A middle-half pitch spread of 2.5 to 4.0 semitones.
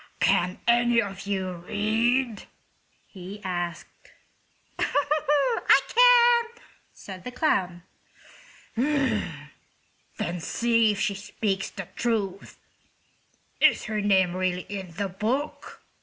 No: average, 4.6 semitones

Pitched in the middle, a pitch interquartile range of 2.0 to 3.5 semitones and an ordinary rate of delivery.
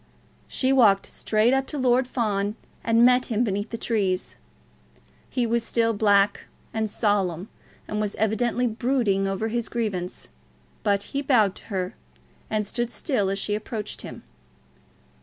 No: high, 220 Hz; average, 3.0 semitones; average, 150 wpm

